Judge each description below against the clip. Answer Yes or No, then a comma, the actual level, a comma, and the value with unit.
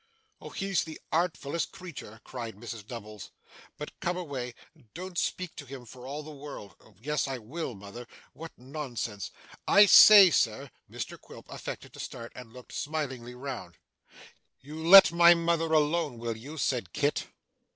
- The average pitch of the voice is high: No, medium, 140 Hz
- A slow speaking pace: No, average, 155 wpm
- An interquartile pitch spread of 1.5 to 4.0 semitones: No, wide, 5.4 semitones